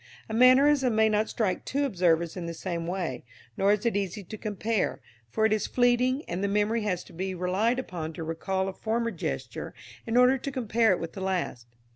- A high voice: Yes, high, 205 Hz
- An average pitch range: Yes, average, 4.5 semitones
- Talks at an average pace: No, fast, 210 wpm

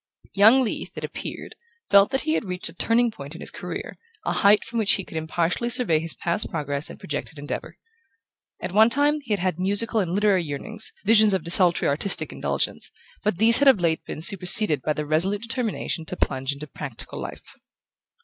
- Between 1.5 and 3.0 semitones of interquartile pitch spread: No, wide, 5.6 semitones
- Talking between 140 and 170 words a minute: No, average, 195 wpm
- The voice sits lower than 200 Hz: Yes, high, 190 Hz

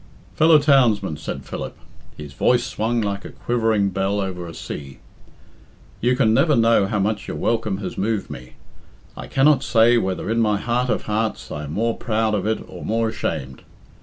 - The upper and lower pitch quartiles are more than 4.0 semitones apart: No, average, 3.3 semitones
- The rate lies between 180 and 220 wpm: Yes, average, 185 wpm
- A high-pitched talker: No, low, 110 Hz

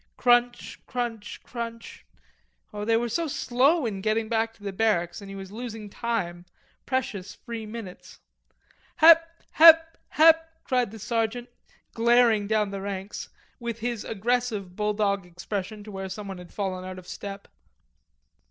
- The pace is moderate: Yes, average, 145 wpm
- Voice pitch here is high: Yes, high, 220 Hz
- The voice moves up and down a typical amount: Yes, average, 3.4 semitones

